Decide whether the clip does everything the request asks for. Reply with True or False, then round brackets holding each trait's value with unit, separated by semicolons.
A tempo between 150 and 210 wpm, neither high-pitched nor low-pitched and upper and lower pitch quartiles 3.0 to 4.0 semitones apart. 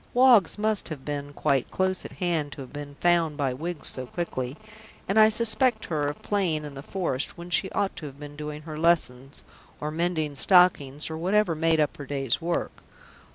True (200 wpm; 155 Hz; 3.7 semitones)